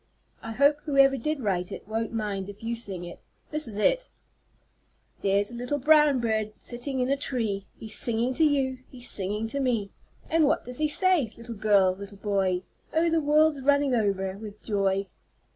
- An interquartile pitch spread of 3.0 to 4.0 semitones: No, wide, 5.6 semitones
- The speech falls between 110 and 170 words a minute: No, average, 190 wpm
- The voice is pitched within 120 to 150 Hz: No, high, 235 Hz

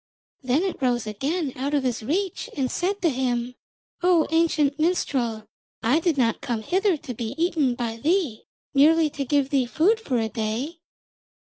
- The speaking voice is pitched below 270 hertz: No, very high, 280 Hz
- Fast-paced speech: No, average, 175 wpm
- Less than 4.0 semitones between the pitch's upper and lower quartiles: No, wide, 5.4 semitones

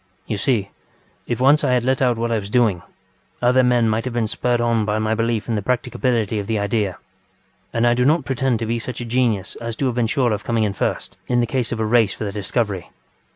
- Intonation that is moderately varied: No, narrow, 2.3 semitones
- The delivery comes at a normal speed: No, fast, 250 wpm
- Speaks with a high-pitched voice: No, low, 115 Hz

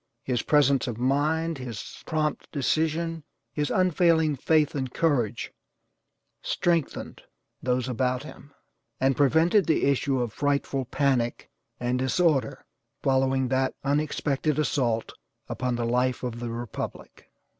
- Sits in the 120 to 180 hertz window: Yes, low, 135 Hz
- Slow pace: Yes, slow, 125 wpm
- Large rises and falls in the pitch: No, average, 3.4 semitones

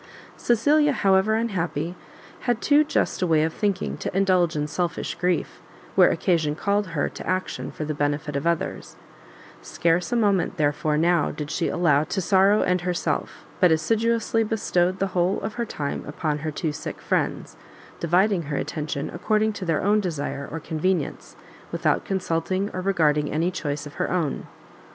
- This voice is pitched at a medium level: Yes, medium, 175 Hz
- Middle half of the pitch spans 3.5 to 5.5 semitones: Yes, average, 4.3 semitones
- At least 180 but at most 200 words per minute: No, average, 170 wpm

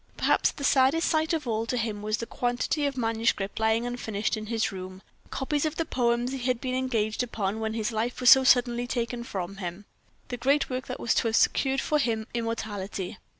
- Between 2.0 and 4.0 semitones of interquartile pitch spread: Yes, average, 3.0 semitones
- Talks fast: Yes, fast, 210 wpm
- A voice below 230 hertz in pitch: No, high, 235 Hz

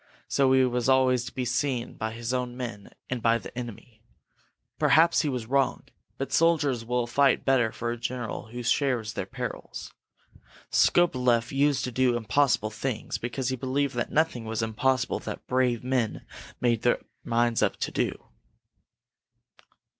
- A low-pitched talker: Yes, low, 125 Hz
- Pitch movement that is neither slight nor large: No, narrow, 2.1 semitones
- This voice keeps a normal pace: Yes, average, 160 wpm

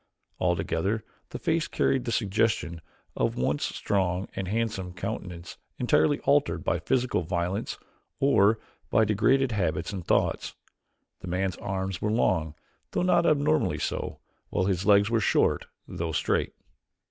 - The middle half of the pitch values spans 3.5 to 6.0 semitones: Yes, average, 4.4 semitones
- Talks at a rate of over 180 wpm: No, average, 140 wpm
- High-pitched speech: No, low, 100 Hz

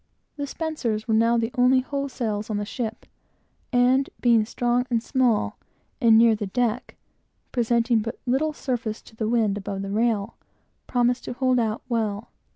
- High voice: Yes, high, 235 Hz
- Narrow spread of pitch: Yes, narrow, 2.3 semitones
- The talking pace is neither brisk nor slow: Yes, average, 165 wpm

